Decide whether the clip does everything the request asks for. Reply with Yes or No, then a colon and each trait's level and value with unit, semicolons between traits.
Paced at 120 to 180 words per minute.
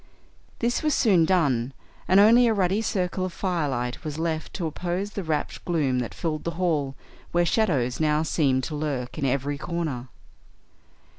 Yes: average, 165 wpm